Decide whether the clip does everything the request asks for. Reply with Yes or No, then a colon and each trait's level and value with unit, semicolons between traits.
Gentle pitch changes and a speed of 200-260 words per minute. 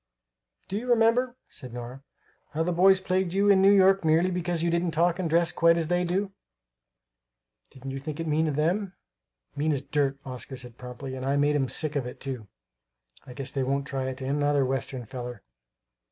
No: average, 5.0 semitones; fast, 205 wpm